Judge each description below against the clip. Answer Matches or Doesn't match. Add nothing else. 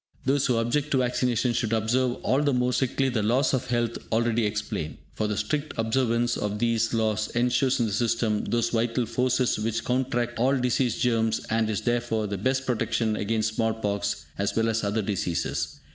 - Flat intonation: Matches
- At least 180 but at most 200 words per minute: Matches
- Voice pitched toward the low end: Matches